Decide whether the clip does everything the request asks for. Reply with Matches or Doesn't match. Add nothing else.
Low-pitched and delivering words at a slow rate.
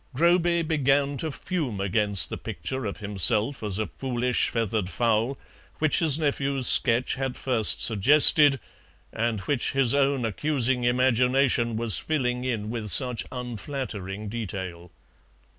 Matches